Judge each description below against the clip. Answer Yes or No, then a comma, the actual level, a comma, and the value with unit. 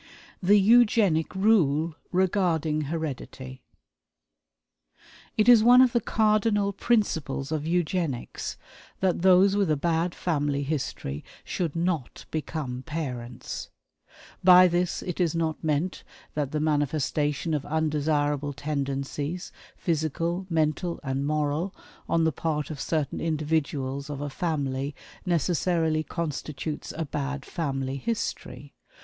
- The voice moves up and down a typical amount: Yes, average, 3.7 semitones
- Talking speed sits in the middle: No, slow, 115 wpm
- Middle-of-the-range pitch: Yes, medium, 155 Hz